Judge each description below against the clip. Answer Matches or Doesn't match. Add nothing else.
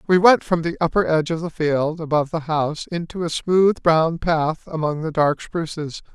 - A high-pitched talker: Doesn't match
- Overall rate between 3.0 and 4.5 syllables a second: Doesn't match